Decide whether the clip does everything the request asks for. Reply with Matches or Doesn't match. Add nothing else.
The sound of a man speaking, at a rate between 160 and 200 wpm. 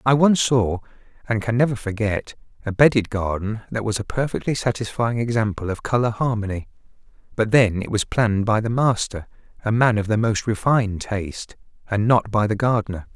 Matches